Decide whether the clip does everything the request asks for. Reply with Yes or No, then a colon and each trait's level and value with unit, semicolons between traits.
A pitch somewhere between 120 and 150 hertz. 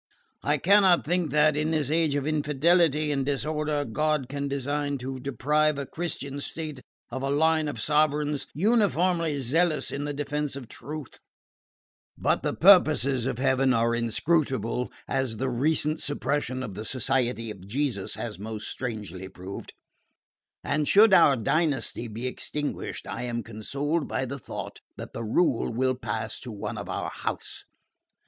Yes: medium, 140 Hz